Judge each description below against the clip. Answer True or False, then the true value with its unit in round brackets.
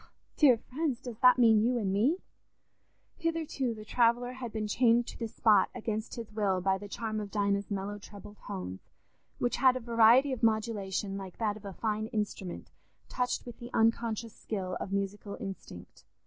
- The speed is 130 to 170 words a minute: False (185 wpm)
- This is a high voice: True (220 Hz)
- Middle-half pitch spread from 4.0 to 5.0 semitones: False (3.0 semitones)